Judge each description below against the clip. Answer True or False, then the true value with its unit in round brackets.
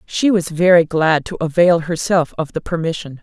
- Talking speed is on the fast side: False (185 wpm)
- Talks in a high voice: False (165 Hz)